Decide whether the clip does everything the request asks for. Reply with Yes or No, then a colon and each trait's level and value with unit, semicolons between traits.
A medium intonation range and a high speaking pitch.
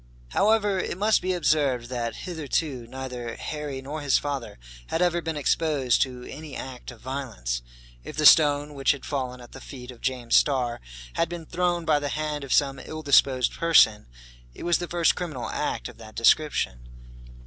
No: average, 4.1 semitones; medium, 140 Hz